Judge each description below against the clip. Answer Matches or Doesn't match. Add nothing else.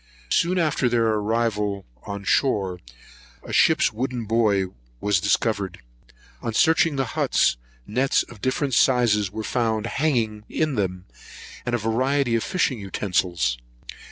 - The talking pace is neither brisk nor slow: Doesn't match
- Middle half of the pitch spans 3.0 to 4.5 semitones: Matches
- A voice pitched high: Doesn't match